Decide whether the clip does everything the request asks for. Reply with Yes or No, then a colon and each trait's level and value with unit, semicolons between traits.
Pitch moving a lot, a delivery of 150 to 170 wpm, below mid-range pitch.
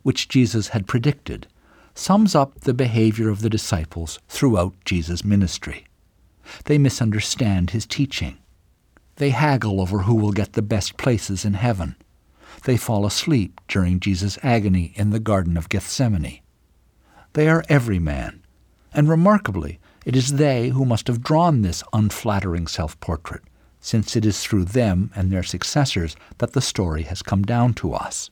Yes: wide, 5.7 semitones; average, 155 wpm; low, 105 Hz